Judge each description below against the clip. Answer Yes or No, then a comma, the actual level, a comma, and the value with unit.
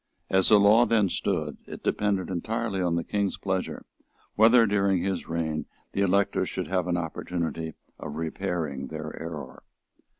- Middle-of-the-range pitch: No, very low, 90 Hz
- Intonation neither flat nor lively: Yes, average, 3.6 semitones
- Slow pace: No, average, 155 wpm